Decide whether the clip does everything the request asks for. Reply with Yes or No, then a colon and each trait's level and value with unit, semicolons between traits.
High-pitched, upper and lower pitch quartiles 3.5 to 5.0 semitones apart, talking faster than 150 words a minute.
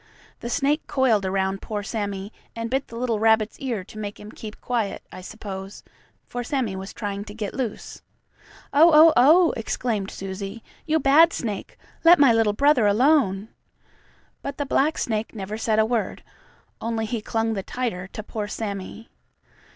Yes: high, 220 Hz; average, 3.8 semitones; average, 165 wpm